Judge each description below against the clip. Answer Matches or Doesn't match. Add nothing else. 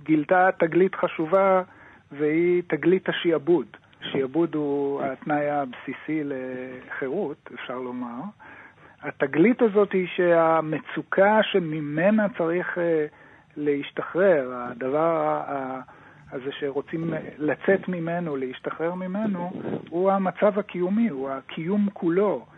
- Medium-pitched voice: Matches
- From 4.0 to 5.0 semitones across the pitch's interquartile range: Matches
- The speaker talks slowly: Matches